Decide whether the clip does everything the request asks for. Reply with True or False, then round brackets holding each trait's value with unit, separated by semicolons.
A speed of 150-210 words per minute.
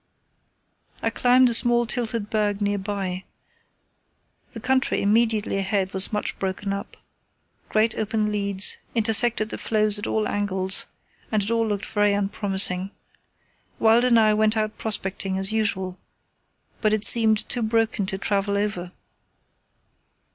False (135 wpm)